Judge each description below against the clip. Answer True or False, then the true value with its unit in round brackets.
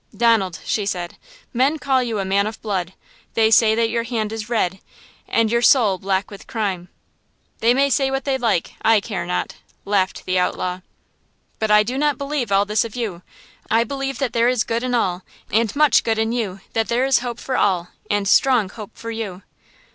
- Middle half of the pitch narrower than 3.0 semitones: False (3.6 semitones)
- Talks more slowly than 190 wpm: False (200 wpm)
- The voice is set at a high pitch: True (225 Hz)